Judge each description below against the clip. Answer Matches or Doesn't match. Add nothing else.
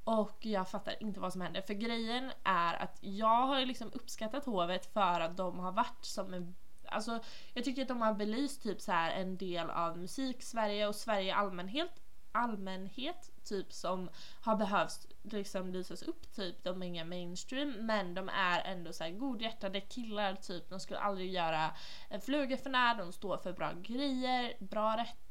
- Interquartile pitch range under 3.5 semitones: Doesn't match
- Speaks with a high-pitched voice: Matches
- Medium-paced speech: Matches